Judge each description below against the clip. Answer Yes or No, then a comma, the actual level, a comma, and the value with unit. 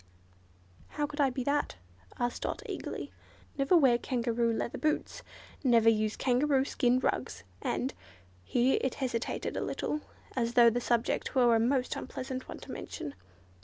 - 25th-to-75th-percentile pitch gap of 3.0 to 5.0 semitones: No, narrow, 2.5 semitones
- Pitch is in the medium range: No, high, 245 Hz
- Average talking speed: Yes, average, 145 wpm